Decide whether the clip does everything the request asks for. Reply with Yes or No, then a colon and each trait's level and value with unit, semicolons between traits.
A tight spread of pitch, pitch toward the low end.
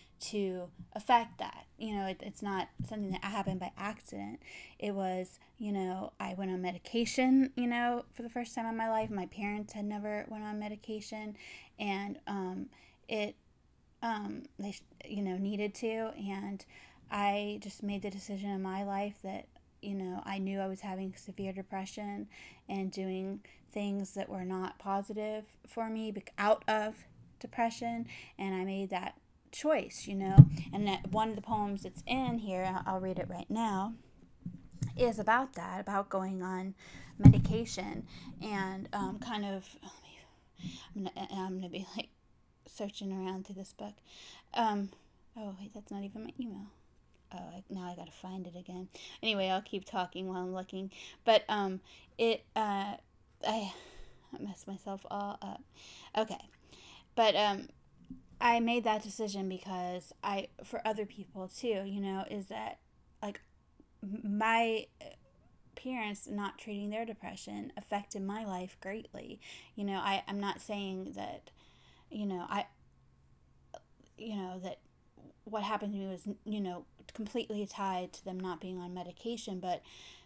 No: narrow, 2.3 semitones; high, 200 Hz